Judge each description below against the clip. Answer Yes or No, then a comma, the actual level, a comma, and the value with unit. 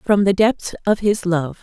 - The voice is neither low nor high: No, high, 195 Hz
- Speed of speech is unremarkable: No, fast, 220 wpm